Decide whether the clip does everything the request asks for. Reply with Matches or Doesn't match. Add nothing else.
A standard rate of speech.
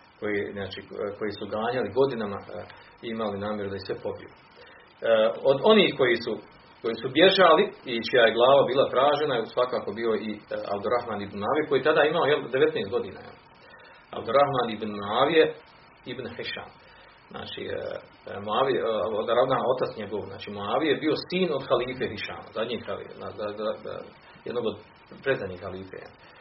Matches